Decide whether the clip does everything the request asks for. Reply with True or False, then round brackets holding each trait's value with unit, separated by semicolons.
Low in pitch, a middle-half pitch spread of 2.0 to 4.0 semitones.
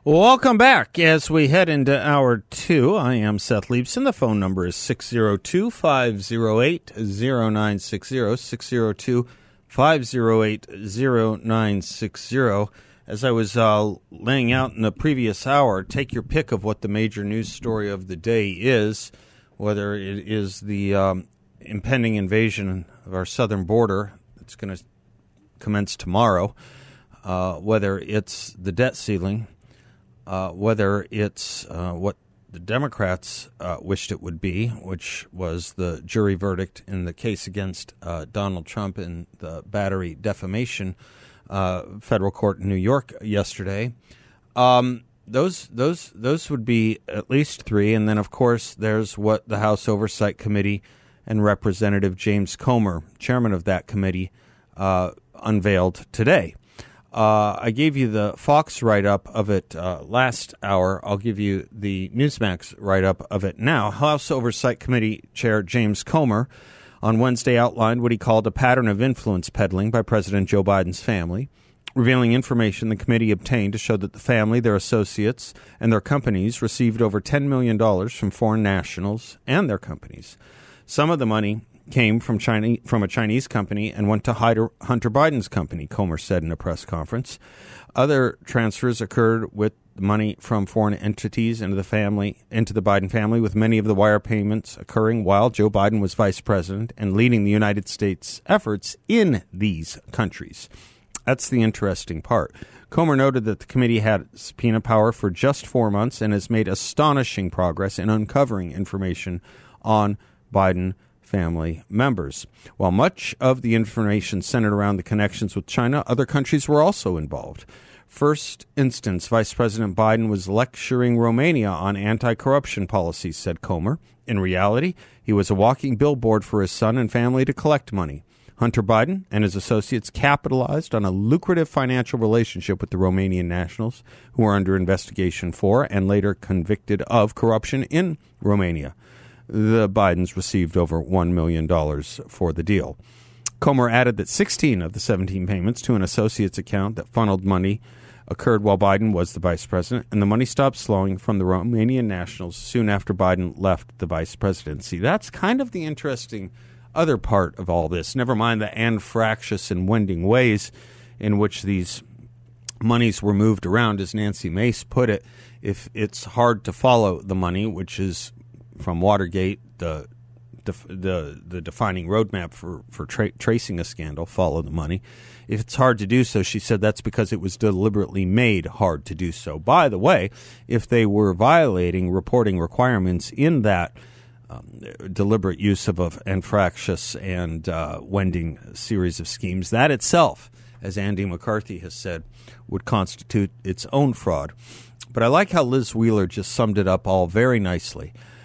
True (110 Hz; 3.6 semitones)